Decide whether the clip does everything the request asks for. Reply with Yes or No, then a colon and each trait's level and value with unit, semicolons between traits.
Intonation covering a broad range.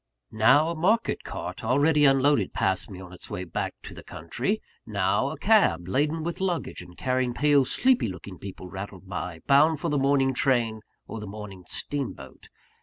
Yes: wide, 7.5 semitones